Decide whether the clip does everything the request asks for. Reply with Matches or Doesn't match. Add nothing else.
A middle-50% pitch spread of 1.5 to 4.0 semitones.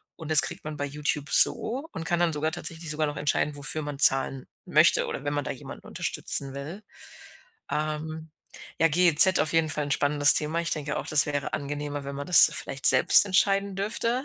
Matches